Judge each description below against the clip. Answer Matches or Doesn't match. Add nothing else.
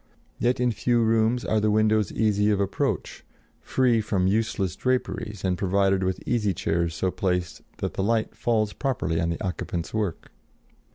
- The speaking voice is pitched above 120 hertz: Doesn't match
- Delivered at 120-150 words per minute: Doesn't match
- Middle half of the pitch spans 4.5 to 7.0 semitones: Doesn't match